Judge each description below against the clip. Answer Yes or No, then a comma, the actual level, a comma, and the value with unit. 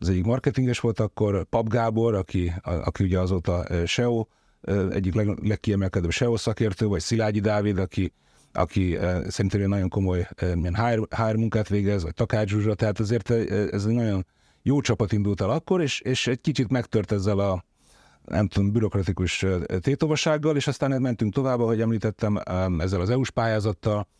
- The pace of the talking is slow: No, fast, 155 wpm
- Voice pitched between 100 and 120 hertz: Yes, low, 105 Hz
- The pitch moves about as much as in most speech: Yes, average, 3.5 semitones